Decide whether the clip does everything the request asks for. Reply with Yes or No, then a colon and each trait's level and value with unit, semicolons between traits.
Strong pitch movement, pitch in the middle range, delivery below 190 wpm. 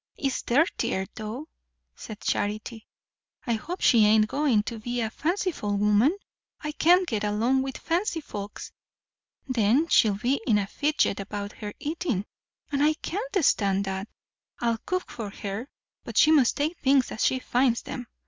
No: wide, 6.1 semitones; high, 240 Hz; average, 160 wpm